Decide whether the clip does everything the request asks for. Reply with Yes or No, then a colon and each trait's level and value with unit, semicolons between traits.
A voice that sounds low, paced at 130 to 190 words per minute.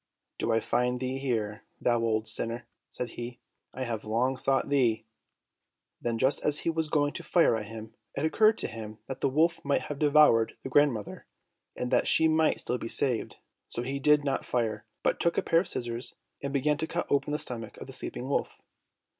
No: low, 130 Hz; fast, 205 wpm